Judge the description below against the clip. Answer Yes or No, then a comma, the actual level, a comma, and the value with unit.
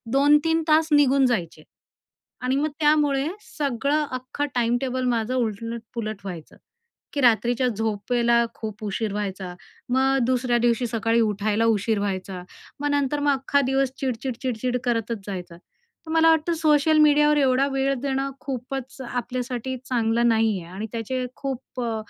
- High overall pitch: Yes, very high, 250 Hz